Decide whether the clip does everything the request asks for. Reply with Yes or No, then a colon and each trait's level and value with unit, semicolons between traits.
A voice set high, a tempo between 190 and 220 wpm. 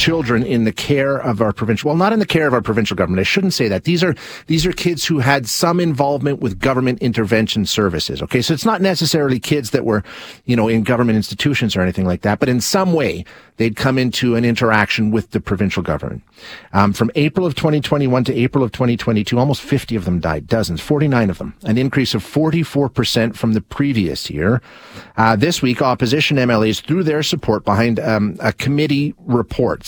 No: low, 125 Hz; fast, 205 wpm